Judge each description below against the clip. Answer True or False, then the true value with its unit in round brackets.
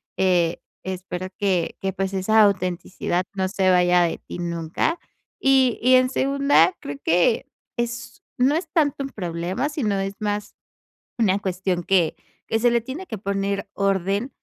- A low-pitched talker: False (195 Hz)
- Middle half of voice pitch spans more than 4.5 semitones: True (4.9 semitones)